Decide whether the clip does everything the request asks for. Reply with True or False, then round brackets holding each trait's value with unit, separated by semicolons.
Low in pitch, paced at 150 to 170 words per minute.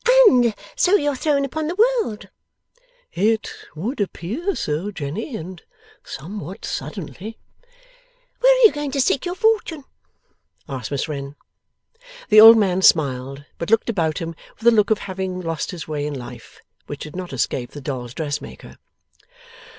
False (195 Hz; 155 wpm)